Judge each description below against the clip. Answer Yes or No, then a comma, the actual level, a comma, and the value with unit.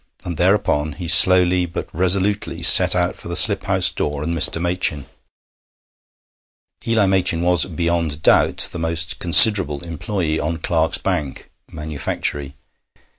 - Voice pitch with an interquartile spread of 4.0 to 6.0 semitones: No, average, 2.9 semitones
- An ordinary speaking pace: No, slow, 130 wpm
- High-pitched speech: No, very low, 85 Hz